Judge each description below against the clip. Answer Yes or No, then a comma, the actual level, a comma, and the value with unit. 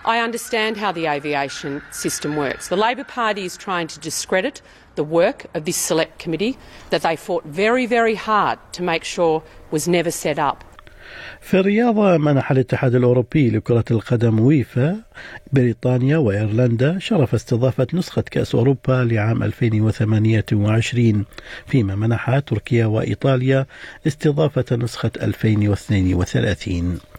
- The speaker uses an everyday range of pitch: No, wide, 6.9 semitones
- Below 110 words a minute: No, average, 125 wpm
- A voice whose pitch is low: Yes, low, 130 Hz